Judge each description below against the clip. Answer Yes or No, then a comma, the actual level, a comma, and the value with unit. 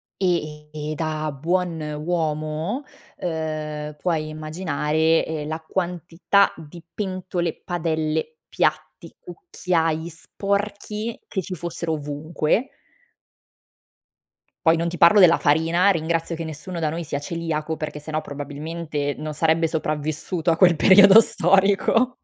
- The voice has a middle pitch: Yes, medium, 165 Hz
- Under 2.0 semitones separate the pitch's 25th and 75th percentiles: No, average, 2.7 semitones